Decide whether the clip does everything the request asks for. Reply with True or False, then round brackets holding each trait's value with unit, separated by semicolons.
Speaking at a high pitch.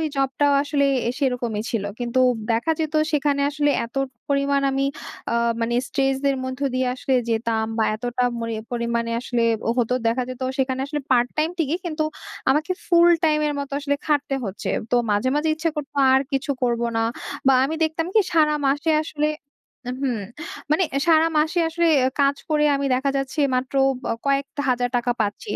True (275 Hz)